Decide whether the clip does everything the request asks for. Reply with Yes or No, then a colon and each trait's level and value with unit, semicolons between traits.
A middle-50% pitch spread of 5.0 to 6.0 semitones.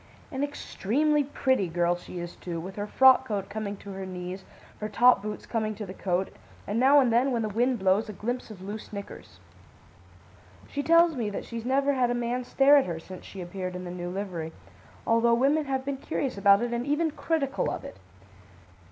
Yes: wide, 5.6 semitones